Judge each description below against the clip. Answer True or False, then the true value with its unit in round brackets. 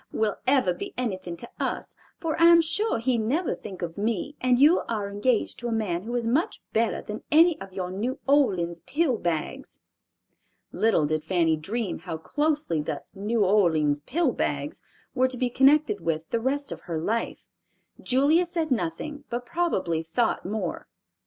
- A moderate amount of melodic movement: False (7.8 semitones)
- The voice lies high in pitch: True (230 Hz)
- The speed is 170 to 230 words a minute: True (175 wpm)